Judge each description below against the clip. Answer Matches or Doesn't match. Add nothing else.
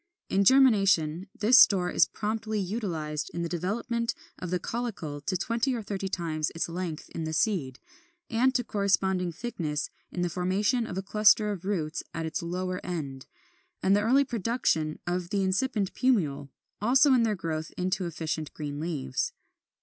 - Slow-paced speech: Doesn't match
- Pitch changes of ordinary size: Matches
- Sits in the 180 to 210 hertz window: Matches